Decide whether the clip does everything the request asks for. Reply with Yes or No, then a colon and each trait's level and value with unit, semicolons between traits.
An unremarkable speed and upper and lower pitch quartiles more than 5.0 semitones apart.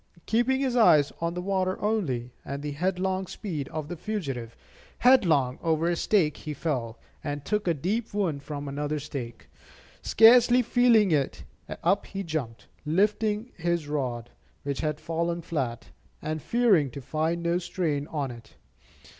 Yes: average, 155 wpm; wide, 5.6 semitones